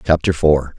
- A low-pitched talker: Yes, very low, 75 Hz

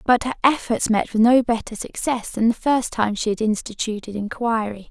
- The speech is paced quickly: No, average, 195 wpm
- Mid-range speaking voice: No, high, 225 Hz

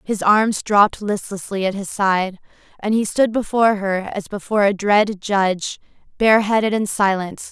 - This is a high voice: Yes, high, 205 Hz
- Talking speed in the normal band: Yes, average, 160 wpm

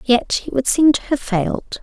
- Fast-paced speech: Yes, fast, 230 wpm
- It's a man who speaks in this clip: No, female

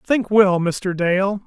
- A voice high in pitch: Yes, high, 195 Hz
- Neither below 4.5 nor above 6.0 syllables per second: No, 3.1 syllables/s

